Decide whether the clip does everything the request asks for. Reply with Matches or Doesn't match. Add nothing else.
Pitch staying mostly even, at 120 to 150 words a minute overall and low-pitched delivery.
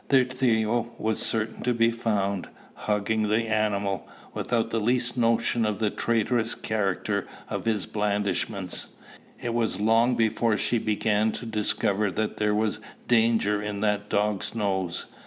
Matches